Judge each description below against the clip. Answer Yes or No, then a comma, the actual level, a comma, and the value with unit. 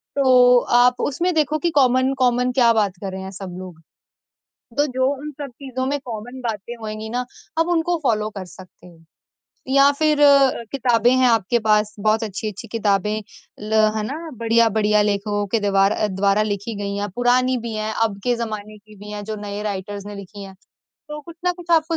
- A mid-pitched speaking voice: No, high, 220 Hz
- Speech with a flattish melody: No, average, 3.9 semitones